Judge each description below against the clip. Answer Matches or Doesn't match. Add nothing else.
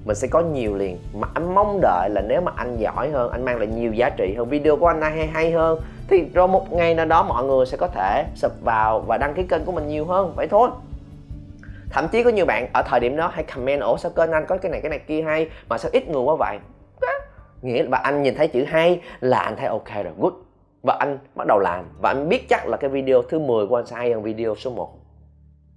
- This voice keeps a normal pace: Doesn't match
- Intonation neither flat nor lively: Doesn't match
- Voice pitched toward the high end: Doesn't match